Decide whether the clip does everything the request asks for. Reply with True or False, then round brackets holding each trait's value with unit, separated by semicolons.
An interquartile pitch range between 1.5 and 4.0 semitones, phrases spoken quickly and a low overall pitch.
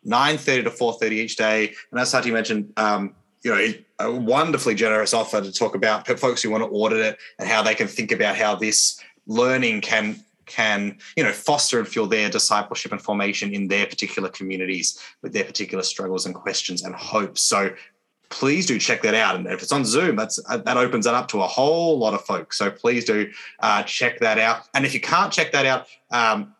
True (3.4 semitones; 220 wpm; 110 Hz)